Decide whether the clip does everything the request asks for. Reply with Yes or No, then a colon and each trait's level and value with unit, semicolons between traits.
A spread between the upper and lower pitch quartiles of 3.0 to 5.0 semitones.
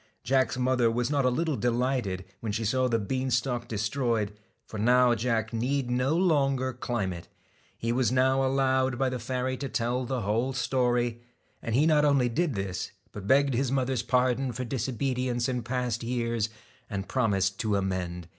No: narrow, 2.5 semitones